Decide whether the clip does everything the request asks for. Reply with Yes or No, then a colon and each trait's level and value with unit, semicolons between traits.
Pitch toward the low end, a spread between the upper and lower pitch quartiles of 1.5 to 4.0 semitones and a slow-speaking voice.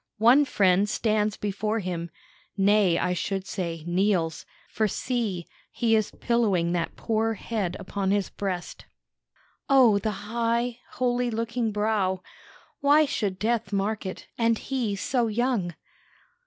No: high, 210 Hz; average, 3.4 semitones; slow, 130 wpm